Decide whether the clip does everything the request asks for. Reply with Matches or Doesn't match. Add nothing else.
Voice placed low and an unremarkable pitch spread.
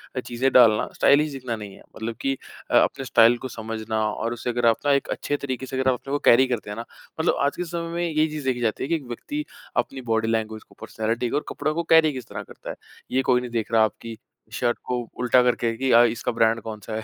Matches